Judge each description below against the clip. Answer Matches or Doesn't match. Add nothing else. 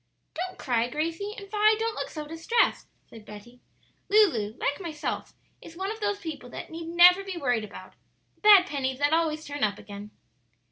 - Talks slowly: Doesn't match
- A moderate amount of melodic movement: Doesn't match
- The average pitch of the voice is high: Matches